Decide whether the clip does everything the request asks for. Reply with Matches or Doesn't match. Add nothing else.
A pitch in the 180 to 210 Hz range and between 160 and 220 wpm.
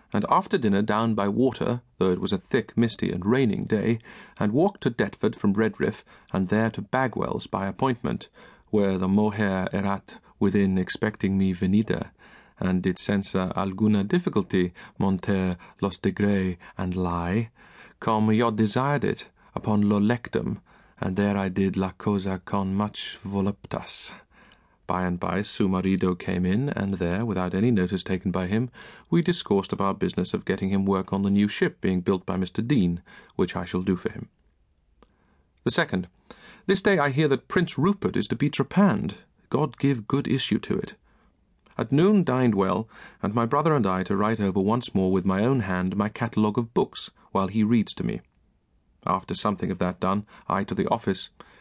Doesn't match